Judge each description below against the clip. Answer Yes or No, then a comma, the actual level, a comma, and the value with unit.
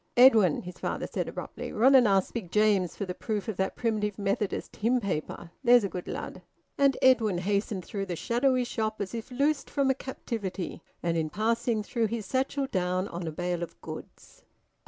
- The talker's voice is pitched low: No, high, 215 Hz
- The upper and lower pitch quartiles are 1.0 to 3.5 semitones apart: No, average, 4.8 semitones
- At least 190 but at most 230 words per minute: Yes, average, 195 wpm